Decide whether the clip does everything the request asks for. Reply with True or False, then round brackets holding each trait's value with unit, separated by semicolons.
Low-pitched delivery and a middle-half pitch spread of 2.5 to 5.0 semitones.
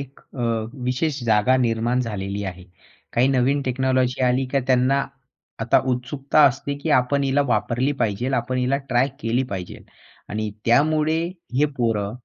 True (125 Hz; 2.9 semitones)